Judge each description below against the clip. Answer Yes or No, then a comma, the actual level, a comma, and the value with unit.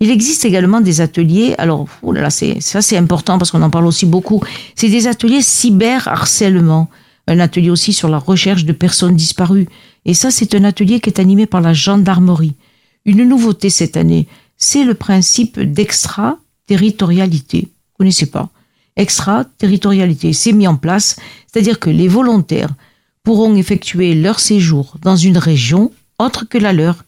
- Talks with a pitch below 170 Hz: No, high, 190 Hz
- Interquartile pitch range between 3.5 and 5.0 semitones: Yes, average, 4.2 semitones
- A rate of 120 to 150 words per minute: No, average, 170 wpm